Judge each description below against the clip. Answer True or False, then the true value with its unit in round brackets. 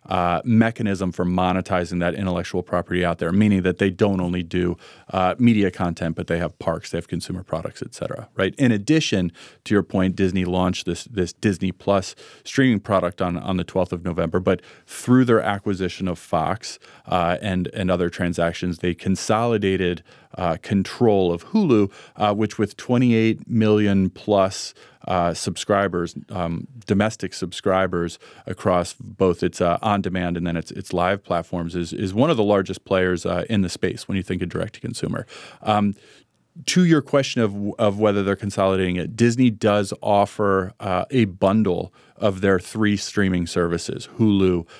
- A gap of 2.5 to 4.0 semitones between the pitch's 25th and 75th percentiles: True (2.8 semitones)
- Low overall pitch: True (95 Hz)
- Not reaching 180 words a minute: True (170 wpm)